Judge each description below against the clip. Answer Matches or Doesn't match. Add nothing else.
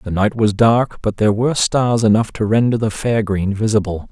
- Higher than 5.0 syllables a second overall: Matches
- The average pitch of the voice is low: Matches